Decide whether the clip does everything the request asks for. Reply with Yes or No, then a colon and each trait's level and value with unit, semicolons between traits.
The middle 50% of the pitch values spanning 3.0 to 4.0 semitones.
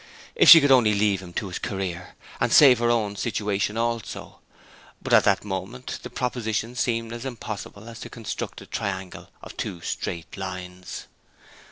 Yes: average, 3.6 semitones